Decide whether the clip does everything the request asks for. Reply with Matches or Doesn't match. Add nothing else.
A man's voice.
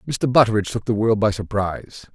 Matches